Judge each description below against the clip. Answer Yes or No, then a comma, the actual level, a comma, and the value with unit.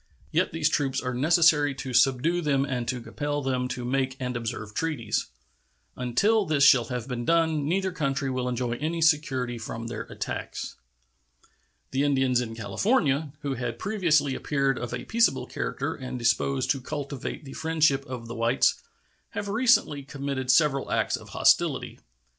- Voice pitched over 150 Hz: No, low, 135 Hz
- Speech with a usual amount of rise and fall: Yes, average, 3.4 semitones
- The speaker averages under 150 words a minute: No, average, 160 wpm